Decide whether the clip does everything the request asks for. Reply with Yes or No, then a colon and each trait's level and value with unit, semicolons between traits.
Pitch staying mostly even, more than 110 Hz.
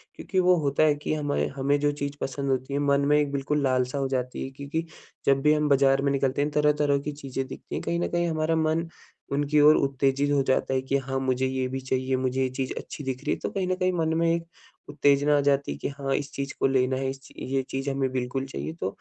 Yes: narrow, 1.9 semitones; medium, 140 Hz